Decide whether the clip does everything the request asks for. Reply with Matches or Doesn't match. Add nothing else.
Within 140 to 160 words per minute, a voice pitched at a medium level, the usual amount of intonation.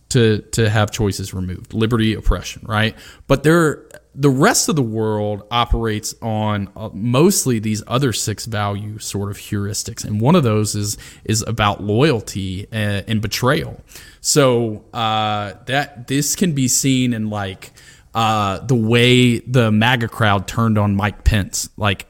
Doesn't match